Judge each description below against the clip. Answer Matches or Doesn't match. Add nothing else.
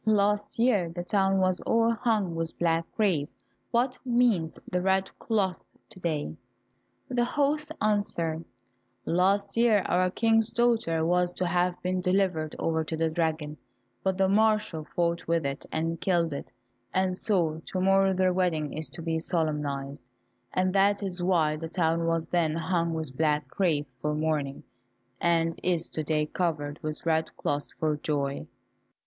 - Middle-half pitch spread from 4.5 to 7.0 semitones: Doesn't match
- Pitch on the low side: Doesn't match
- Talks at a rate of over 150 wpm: Matches